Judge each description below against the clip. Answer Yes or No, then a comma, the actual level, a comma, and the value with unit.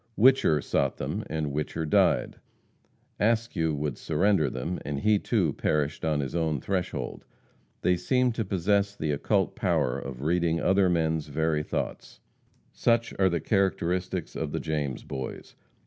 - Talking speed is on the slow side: No, average, 145 wpm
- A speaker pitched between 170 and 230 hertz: No, very low, 80 Hz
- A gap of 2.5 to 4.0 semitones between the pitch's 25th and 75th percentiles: No, average, 4.5 semitones